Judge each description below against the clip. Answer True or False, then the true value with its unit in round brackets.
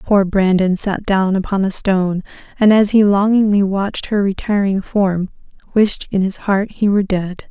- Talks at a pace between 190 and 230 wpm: False (175 wpm)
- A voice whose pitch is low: False (195 Hz)